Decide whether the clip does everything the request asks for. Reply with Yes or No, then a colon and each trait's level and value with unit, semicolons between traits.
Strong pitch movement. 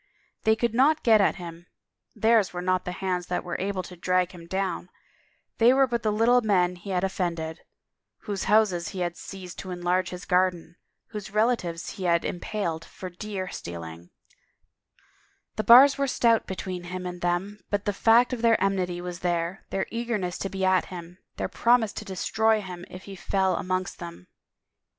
No: average, 3.3 semitones